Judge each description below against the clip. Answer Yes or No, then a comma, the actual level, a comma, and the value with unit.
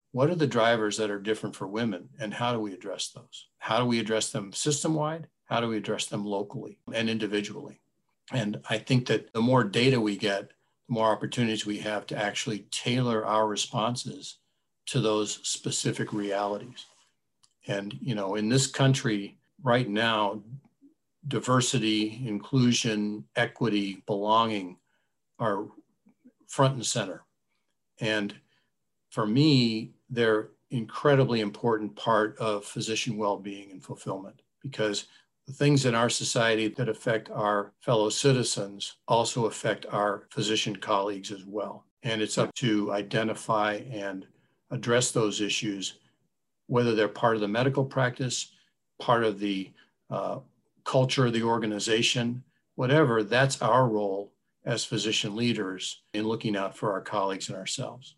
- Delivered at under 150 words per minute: Yes, average, 140 wpm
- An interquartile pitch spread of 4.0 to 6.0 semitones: No, average, 3.4 semitones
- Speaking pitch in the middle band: No, low, 110 Hz